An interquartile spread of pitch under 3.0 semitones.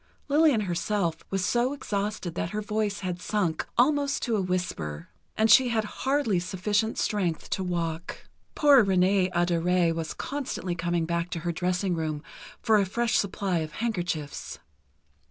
No: average, 4.0 semitones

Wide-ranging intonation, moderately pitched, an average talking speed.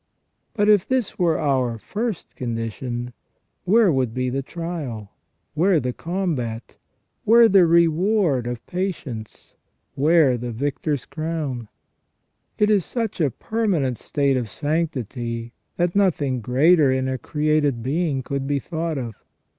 No: wide, 5.8 semitones; medium, 145 Hz; slow, 130 wpm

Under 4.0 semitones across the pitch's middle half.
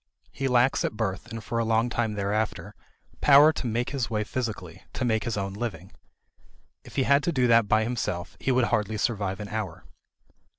Yes: average, 2.9 semitones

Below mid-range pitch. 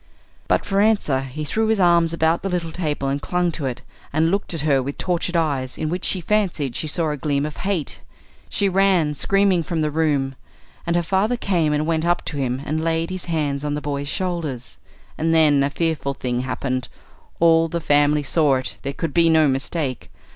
No: medium, 160 Hz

